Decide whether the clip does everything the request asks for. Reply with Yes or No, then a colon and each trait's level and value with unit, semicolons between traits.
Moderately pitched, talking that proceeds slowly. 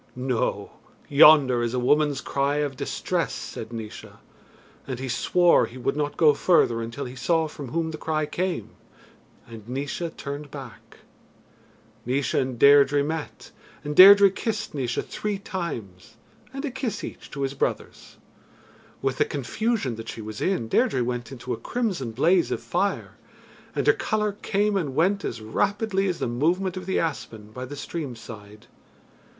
No: medium, 145 Hz; average, 165 wpm